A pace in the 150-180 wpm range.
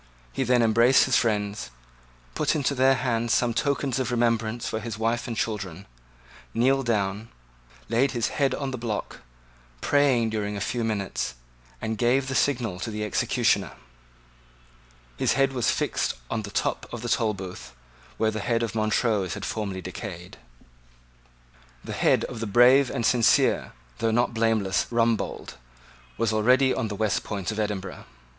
Yes: average, 160 wpm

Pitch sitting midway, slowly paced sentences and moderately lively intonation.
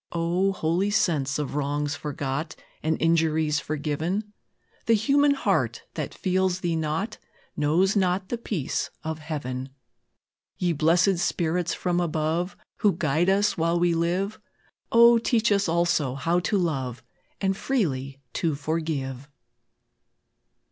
Yes: medium, 165 Hz; slow, 125 wpm; average, 4.2 semitones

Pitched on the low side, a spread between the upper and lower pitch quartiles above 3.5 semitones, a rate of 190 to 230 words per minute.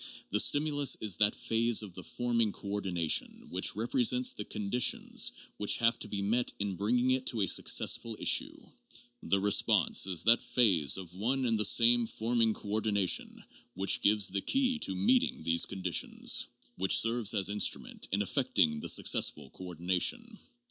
No: low, 105 Hz; average, 3.9 semitones; average, 160 wpm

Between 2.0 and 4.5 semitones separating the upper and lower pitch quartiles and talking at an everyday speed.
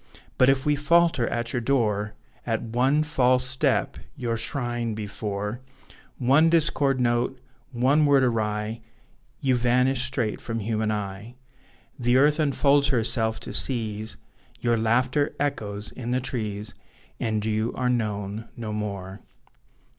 No: average, 3.4 semitones; slow, 130 wpm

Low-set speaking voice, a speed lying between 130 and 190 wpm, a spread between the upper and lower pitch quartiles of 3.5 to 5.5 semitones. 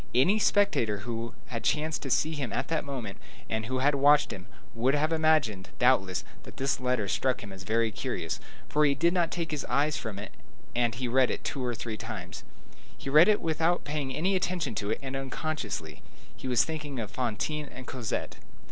No: low, 130 Hz; average, 200 wpm; average, 5.1 semitones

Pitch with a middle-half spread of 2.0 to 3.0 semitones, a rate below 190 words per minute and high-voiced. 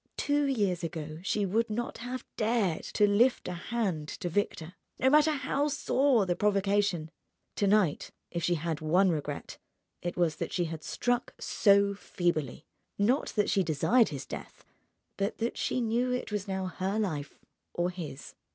No: average, 5.3 semitones; average, 165 wpm; high, 200 Hz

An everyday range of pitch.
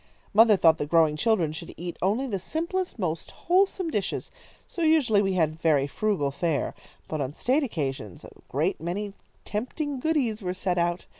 No: wide, 7.6 semitones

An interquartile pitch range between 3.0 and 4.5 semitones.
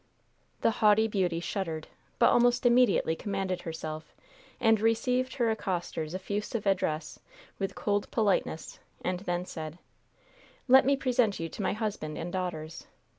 No: average, 4.9 semitones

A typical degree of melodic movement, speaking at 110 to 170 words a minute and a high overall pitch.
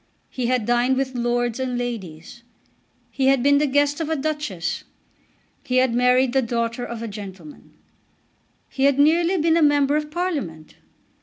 Yes: average, 3.6 semitones; average, 165 wpm; very high, 255 Hz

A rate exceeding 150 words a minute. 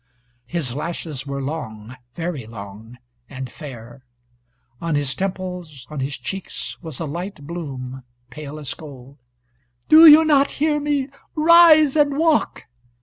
No: slow, 135 wpm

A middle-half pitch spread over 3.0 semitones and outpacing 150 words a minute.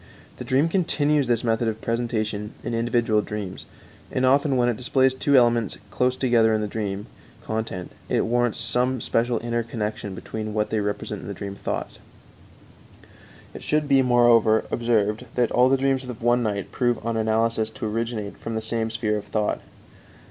No: narrow, 2.4 semitones; average, 175 wpm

